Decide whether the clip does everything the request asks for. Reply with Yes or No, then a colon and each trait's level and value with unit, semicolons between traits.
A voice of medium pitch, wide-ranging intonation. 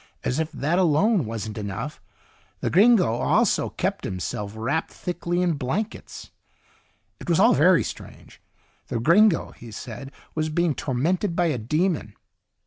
Yes: medium, 155 Hz; wide, 6.8 semitones